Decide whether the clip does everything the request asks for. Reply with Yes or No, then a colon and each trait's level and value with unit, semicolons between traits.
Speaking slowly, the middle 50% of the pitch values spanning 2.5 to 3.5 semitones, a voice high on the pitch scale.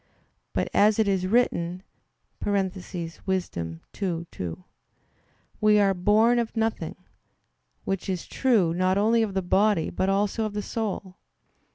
Yes: slow, 130 wpm; average, 2.9 semitones; high, 195 Hz